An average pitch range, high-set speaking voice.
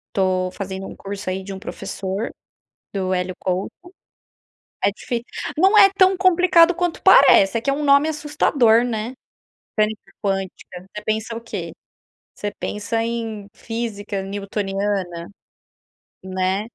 Yes: average, 3.8 semitones; high, 210 Hz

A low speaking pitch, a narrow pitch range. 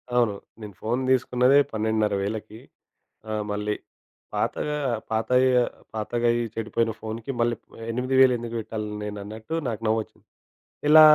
Yes: low, 110 Hz; narrow, 2.1 semitones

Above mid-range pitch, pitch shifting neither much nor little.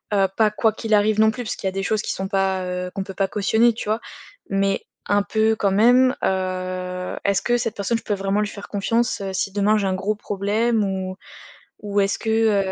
No: high, 200 Hz; narrow, 2.1 semitones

